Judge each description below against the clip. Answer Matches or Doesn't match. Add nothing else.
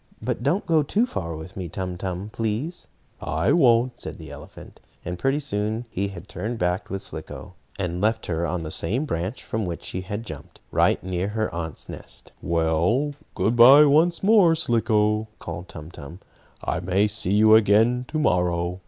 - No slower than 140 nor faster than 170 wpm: Doesn't match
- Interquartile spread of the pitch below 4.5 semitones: Doesn't match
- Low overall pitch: Matches